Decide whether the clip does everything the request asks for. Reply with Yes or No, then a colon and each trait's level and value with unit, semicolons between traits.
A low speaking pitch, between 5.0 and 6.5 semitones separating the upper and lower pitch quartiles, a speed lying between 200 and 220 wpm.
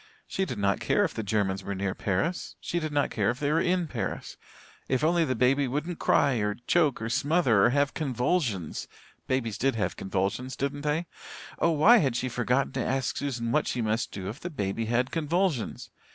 Yes: low, 130 Hz; average, 5.3 semitones; fast, 205 wpm